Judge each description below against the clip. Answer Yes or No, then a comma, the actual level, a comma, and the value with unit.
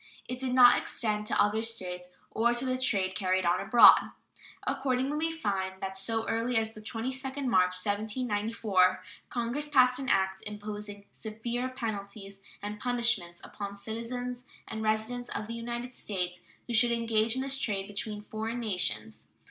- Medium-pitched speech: No, high, 220 Hz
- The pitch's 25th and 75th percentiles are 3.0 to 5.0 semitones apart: Yes, average, 3.5 semitones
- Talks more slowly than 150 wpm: No, average, 155 wpm